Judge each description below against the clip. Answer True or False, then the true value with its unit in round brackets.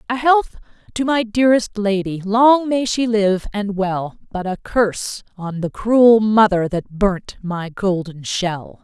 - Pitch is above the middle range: True (210 Hz)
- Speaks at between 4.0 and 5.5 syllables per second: False (3.8 syllables/s)